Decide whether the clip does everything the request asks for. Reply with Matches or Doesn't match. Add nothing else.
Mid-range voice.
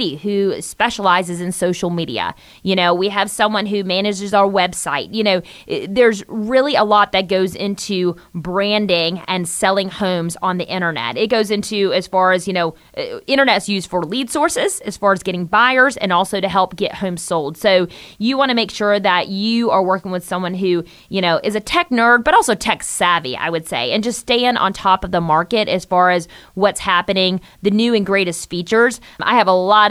Doesn't match